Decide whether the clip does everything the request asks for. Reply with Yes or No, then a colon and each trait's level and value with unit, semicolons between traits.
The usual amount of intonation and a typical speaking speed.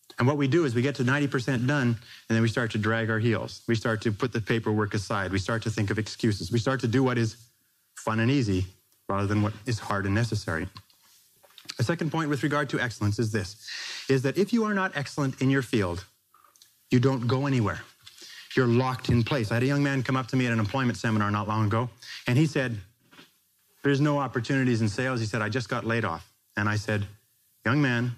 No: average, 3.6 semitones; fast, 235 wpm